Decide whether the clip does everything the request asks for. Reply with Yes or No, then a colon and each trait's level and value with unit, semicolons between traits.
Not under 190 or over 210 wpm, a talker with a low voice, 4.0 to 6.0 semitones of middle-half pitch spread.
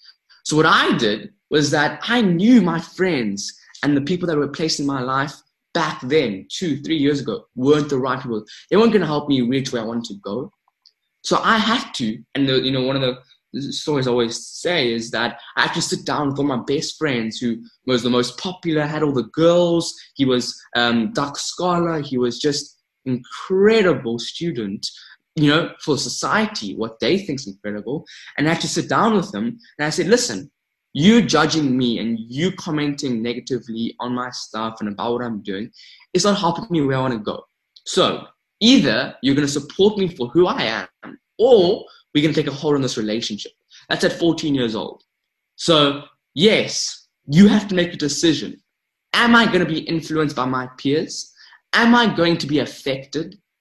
No: average, 200 wpm; medium, 145 Hz; average, 5.3 semitones